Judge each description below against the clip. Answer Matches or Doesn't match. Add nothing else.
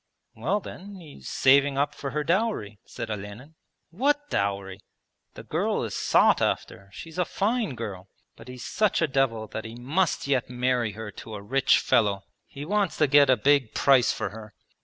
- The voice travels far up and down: Matches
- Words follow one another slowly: Doesn't match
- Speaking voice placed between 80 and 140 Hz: Matches